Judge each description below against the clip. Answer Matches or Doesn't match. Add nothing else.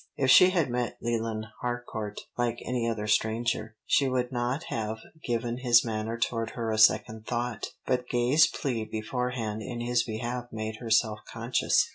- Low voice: Matches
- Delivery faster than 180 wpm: Doesn't match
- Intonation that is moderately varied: Doesn't match